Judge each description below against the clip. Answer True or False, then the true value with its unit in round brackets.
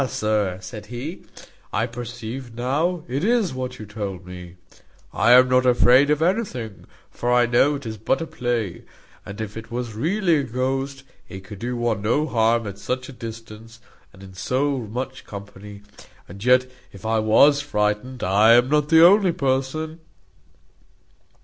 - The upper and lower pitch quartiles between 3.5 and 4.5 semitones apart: True (4.0 semitones)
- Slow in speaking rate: False (170 wpm)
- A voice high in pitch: False (120 Hz)